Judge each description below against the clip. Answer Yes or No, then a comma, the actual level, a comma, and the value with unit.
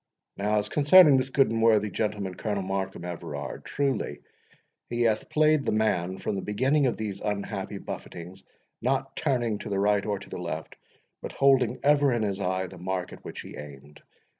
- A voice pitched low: Yes, low, 105 Hz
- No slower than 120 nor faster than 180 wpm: No, average, 190 wpm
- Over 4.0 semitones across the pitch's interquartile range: Yes, average, 4.8 semitones